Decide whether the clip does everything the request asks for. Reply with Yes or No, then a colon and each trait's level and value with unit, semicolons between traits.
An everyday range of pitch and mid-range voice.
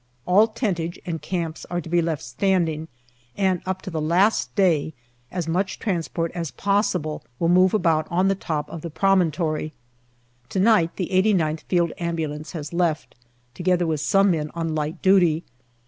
Yes: average, 3.0 semitones; medium, 170 Hz